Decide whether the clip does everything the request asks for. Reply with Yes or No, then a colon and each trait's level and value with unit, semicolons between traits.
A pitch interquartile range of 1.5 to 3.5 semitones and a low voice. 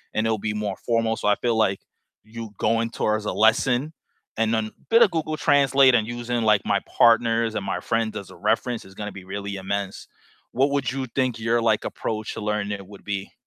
Yes: narrow, 2.6 semitones; low, 110 Hz